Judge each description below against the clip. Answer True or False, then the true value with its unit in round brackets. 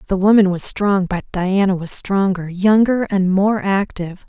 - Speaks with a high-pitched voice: True (195 Hz)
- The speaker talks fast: False (170 wpm)